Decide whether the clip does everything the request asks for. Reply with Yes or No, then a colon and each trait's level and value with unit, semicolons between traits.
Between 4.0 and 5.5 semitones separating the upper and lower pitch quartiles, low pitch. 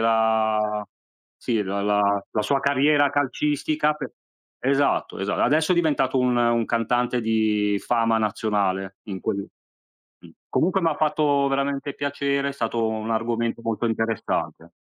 Yes: average, 4.3 semitones; low, 115 Hz